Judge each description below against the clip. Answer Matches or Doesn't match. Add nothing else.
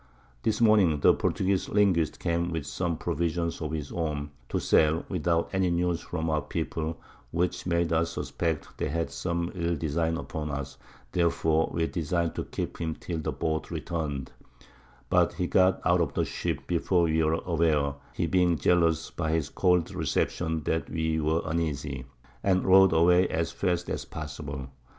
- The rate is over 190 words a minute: Doesn't match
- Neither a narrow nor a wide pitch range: Doesn't match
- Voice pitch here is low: Matches